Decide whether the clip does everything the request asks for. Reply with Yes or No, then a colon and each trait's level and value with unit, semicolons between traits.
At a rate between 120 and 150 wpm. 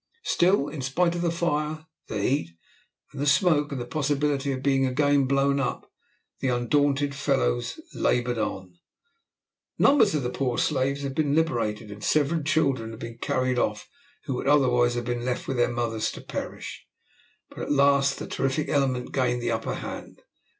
No: average, 175 wpm